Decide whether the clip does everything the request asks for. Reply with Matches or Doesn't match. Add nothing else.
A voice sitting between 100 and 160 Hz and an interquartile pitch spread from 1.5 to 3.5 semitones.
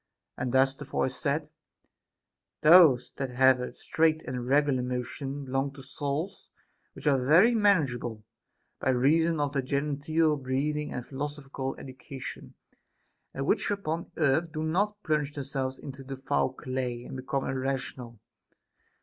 Matches